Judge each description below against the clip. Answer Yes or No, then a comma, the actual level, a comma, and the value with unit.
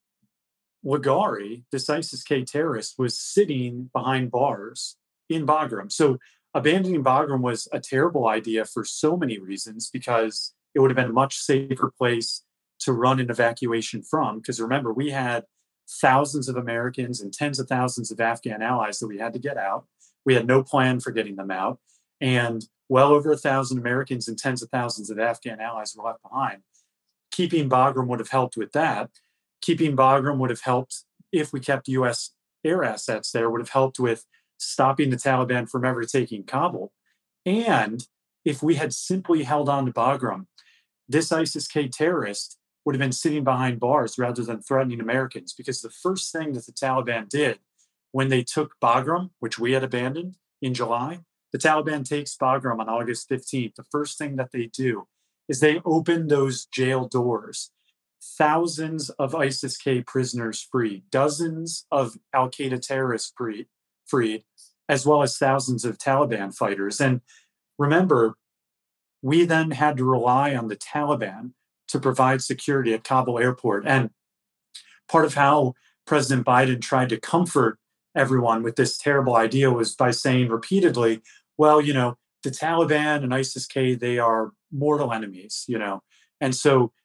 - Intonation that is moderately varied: Yes, average, 3.5 semitones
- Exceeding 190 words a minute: No, average, 165 wpm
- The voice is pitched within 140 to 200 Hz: No, low, 130 Hz